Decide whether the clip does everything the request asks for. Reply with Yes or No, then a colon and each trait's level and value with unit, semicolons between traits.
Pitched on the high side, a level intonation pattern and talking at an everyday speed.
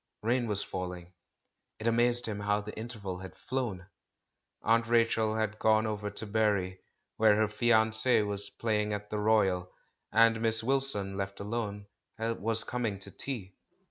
No: low, 110 Hz; narrow, 2.2 semitones; average, 160 wpm